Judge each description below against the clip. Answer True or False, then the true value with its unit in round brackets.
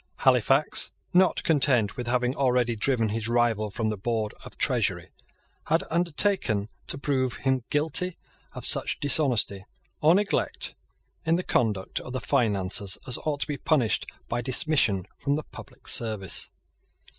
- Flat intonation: False (4.8 semitones)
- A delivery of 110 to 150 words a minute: True (145 wpm)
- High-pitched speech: False (125 Hz)